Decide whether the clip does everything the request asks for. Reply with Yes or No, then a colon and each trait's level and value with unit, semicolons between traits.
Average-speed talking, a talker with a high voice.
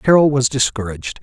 No: average, 145 wpm; low, 125 Hz